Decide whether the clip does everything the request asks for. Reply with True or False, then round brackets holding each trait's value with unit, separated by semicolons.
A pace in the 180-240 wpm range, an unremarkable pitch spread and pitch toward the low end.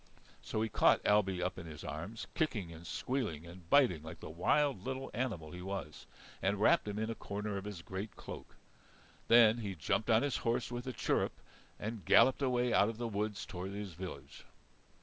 True (195 wpm; 4.7 semitones; 105 Hz)